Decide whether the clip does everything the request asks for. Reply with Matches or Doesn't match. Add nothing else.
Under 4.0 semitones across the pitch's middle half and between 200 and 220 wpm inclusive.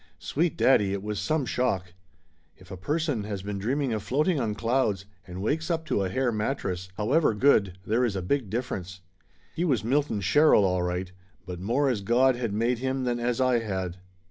Doesn't match